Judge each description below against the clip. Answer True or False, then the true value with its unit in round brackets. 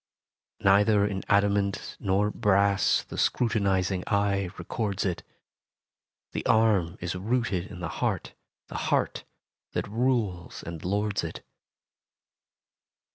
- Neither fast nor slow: False (110 wpm)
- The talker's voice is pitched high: False (100 Hz)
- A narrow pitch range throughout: True (2.0 semitones)